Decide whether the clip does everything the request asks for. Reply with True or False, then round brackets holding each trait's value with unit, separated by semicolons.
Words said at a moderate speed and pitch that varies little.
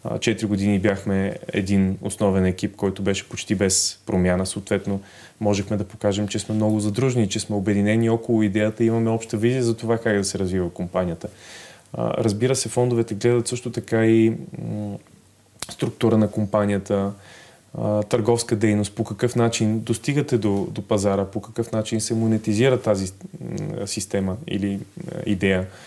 True (145 wpm; 2.3 semitones)